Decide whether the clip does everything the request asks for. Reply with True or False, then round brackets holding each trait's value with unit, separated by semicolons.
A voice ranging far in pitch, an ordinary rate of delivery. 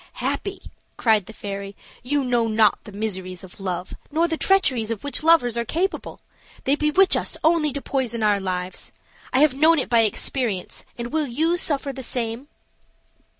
True (6.1 semitones; 175 wpm)